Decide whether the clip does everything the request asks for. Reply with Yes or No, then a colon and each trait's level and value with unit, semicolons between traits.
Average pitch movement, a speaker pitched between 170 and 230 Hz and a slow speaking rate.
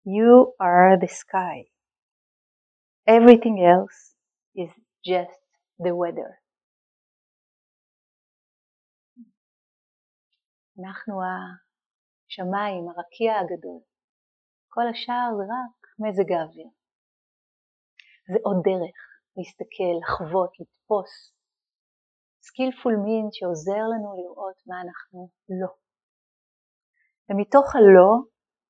Yes: average, 4.0 semitones; high, 190 Hz; slow, 75 wpm